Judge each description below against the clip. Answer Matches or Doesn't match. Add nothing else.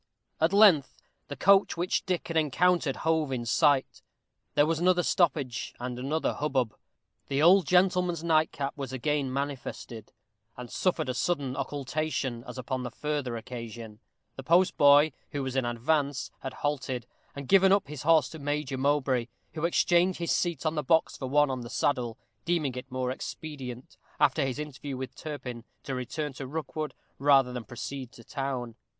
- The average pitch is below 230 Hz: Matches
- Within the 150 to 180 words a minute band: Matches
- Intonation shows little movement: Doesn't match